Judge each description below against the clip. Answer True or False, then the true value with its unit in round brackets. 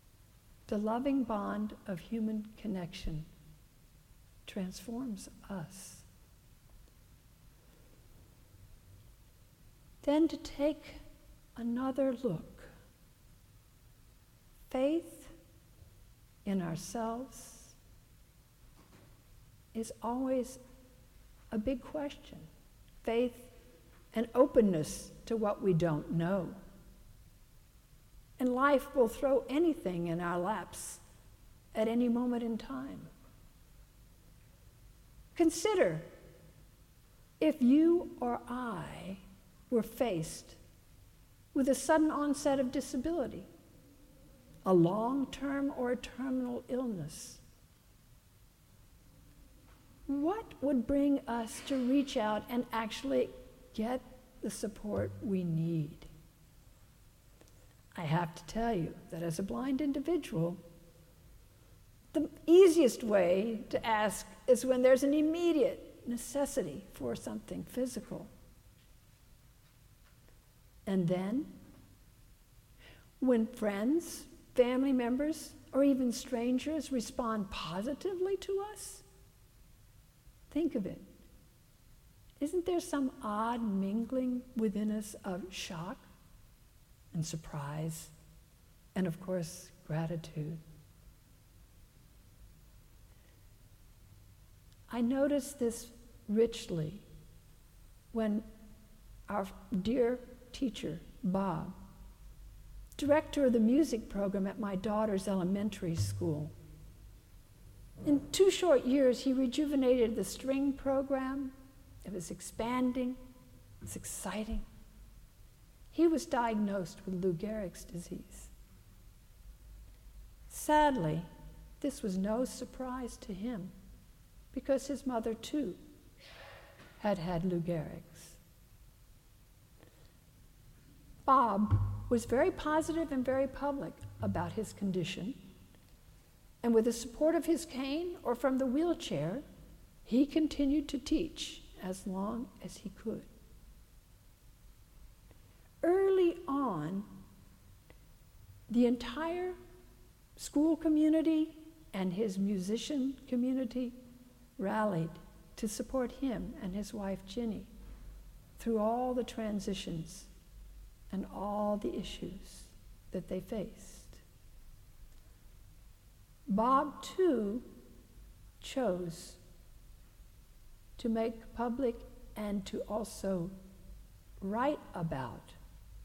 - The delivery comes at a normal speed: False (85 wpm)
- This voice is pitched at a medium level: False (220 Hz)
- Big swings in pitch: True (8.5 semitones)